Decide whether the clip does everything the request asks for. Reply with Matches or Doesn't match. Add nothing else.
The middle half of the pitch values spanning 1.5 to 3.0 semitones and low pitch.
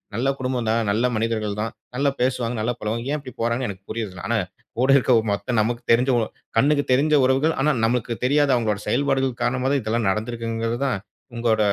Matches